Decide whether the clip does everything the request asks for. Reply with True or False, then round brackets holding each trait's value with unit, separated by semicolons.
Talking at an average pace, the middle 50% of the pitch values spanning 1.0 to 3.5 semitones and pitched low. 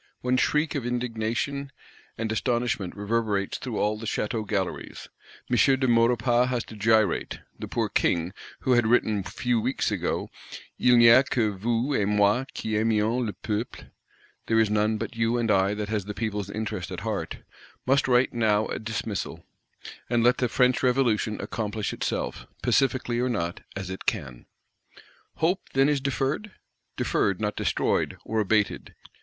True (160 wpm; 2.8 semitones; 115 Hz)